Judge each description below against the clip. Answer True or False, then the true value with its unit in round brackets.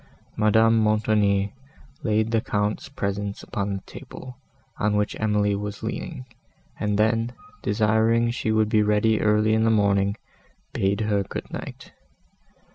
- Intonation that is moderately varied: False (1.4 semitones)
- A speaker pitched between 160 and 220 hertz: False (105 Hz)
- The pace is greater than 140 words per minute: False (135 wpm)